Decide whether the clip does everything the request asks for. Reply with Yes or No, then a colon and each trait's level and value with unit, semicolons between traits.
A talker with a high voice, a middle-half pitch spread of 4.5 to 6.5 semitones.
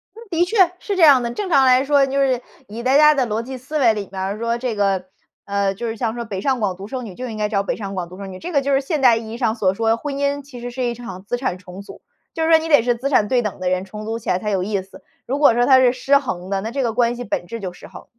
Yes: high, 235 Hz; average, 5.1 semitones